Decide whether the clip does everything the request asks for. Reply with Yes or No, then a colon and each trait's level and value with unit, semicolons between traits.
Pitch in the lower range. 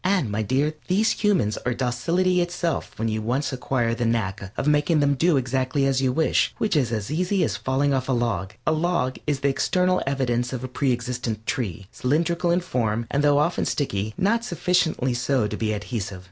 Yes: low, 130 Hz